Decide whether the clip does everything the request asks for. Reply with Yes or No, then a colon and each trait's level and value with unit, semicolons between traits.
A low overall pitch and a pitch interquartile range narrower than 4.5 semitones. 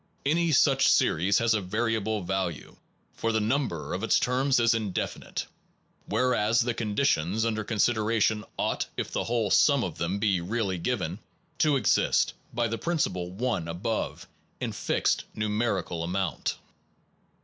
Yes: low, 110 Hz; average, 4.0 semitones